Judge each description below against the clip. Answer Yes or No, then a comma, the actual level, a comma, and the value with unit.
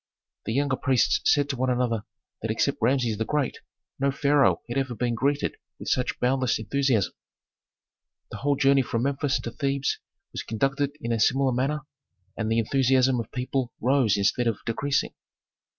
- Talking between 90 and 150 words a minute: No, average, 165 wpm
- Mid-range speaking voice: No, low, 130 Hz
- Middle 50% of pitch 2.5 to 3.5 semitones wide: Yes, average, 2.9 semitones